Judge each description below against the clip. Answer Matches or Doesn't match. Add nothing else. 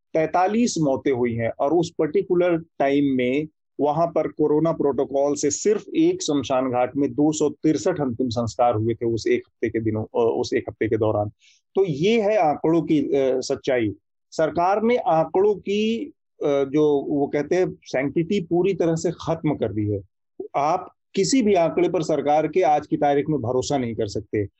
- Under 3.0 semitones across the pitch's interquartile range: Doesn't match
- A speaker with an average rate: Matches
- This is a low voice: Doesn't match